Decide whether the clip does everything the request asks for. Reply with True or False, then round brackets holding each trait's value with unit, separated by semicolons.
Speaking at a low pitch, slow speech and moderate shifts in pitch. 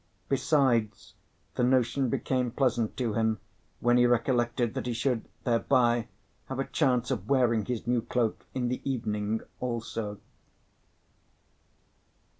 False (120 Hz; 125 wpm; 2.0 semitones)